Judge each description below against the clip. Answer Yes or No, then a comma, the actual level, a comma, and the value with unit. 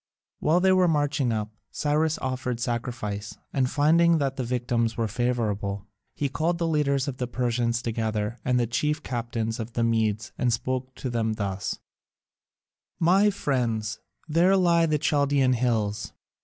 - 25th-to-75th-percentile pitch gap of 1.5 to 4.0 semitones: No, average, 4.5 semitones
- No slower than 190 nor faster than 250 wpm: No, average, 155 wpm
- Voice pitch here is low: Yes, low, 125 Hz